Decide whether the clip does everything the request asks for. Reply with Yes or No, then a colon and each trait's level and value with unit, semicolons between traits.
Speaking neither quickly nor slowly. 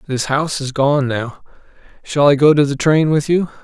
No: fast, 215 wpm